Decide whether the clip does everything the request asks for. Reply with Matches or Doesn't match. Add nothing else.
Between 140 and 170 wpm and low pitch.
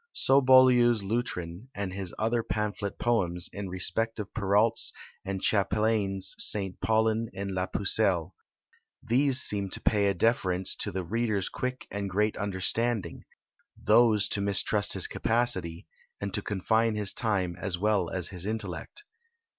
Matches